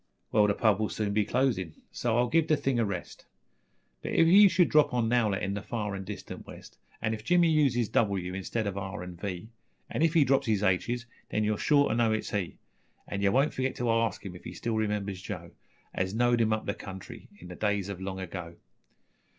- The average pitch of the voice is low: Yes, low, 110 Hz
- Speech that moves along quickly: Yes, fast, 230 wpm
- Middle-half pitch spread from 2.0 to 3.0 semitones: No, average, 3.8 semitones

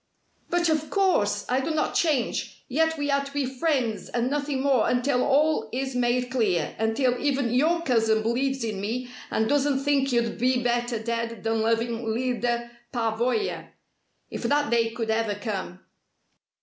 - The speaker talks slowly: No, average, 160 wpm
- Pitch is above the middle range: Yes, high, 245 Hz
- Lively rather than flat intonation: No, average, 3.5 semitones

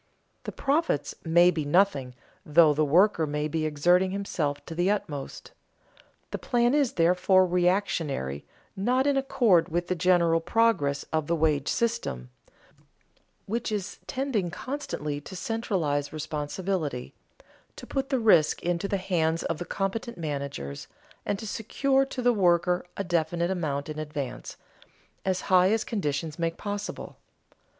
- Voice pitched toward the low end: No, medium, 175 Hz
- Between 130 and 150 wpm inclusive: Yes, average, 140 wpm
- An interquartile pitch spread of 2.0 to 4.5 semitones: No, average, 5.1 semitones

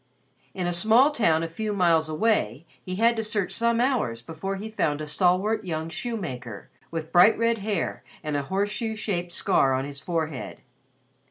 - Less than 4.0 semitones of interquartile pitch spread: No, wide, 5.6 semitones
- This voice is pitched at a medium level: Yes, medium, 180 Hz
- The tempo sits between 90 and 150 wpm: No, average, 175 wpm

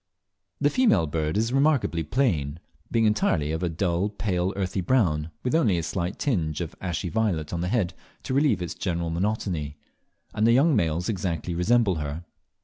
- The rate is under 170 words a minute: No, average, 175 wpm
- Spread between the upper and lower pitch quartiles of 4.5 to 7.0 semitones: Yes, average, 5.2 semitones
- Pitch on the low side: Yes, very low, 90 Hz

